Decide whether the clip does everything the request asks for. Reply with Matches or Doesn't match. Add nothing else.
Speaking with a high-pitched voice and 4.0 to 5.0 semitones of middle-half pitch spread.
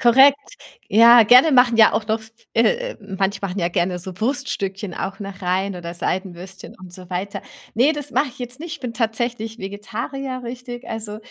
Matches